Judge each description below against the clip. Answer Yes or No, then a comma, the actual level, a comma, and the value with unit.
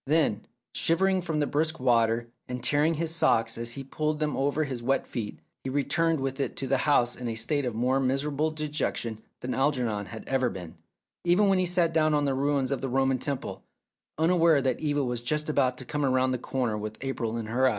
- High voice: No, low, 135 Hz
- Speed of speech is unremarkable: No, fast, 220 wpm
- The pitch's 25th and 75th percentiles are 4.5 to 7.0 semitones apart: No, average, 3.7 semitones